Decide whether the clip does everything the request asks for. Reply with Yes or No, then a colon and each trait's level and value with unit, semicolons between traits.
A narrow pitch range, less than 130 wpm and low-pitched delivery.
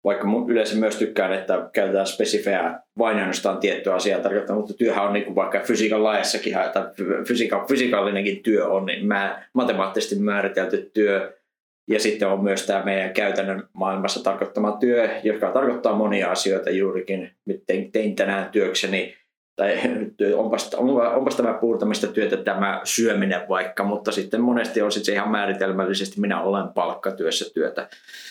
No: narrow, 1.9 semitones; average, 145 wpm; low, 100 Hz